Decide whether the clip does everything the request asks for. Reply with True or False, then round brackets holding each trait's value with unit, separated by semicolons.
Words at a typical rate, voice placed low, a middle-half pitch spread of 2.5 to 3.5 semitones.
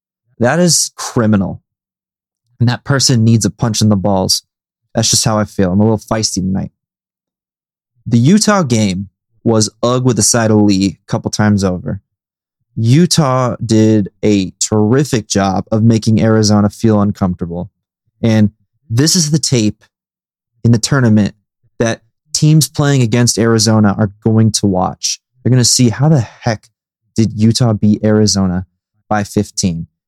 True (150 wpm; 110 Hz; 2.9 semitones)